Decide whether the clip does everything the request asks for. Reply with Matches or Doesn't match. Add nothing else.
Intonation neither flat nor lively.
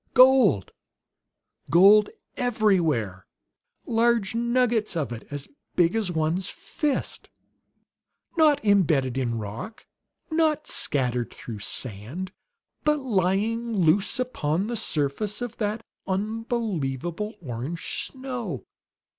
Doesn't match